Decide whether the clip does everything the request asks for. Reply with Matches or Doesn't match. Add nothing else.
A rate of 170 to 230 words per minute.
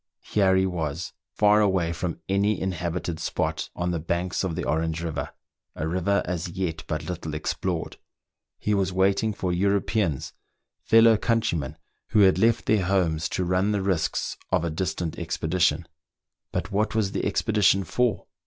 Doesn't match